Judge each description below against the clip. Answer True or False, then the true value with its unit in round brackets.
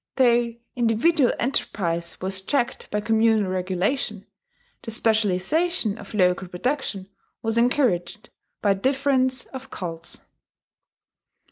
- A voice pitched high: True (220 Hz)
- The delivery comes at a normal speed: False (100 wpm)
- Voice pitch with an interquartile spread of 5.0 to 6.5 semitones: True (5.3 semitones)